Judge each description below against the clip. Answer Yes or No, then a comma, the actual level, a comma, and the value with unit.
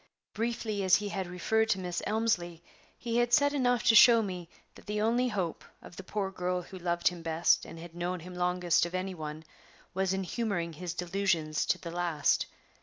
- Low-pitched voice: No, medium, 185 Hz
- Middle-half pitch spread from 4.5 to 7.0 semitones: No, average, 3.7 semitones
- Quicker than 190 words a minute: Yes, average, 200 wpm